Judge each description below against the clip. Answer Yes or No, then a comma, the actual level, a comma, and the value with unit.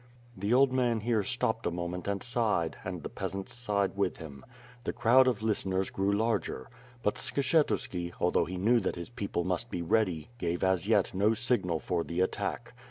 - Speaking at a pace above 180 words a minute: Yes, average, 190 wpm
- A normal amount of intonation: Yes, average, 4.7 semitones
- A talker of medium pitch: No, low, 100 Hz